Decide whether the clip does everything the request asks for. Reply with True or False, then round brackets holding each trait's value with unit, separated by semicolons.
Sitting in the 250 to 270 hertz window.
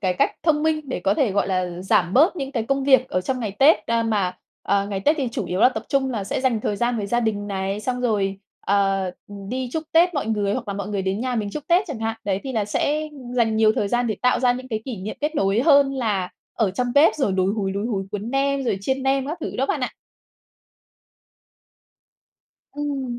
False (225 Hz)